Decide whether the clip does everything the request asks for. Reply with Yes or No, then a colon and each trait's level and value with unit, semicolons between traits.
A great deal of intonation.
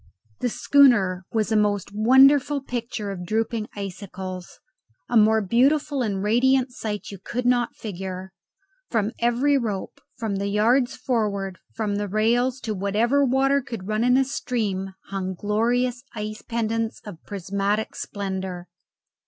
No: average, 3.7 semitones